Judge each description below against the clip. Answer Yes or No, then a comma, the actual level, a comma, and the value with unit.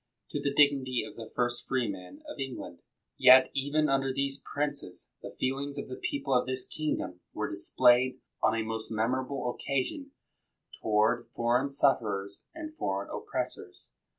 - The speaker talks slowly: No, average, 150 wpm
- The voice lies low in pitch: Yes, low, 130 Hz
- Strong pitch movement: No, average, 3.6 semitones